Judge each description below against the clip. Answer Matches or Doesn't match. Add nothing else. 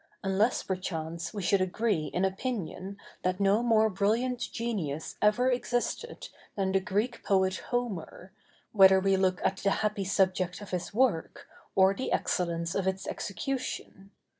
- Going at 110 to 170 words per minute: Matches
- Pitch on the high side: Matches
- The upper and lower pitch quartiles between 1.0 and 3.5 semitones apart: Matches